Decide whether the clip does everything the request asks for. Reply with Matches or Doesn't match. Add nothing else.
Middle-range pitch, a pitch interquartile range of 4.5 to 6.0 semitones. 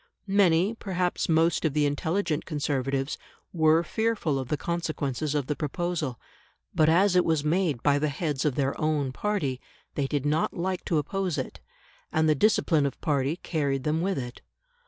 Doesn't match